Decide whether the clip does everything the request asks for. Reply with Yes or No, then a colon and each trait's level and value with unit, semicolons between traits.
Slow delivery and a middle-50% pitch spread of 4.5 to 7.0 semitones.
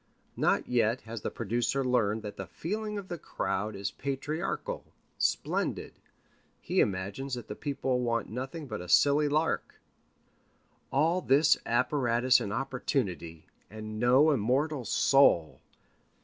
Yes: slow, 125 wpm; average, 5.0 semitones